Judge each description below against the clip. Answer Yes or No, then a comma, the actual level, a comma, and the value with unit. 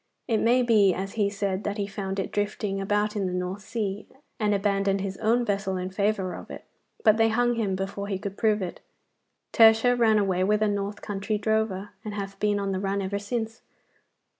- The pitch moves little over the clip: Yes, narrow, 1.8 semitones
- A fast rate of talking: Yes, fast, 210 wpm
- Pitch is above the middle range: Yes, high, 205 Hz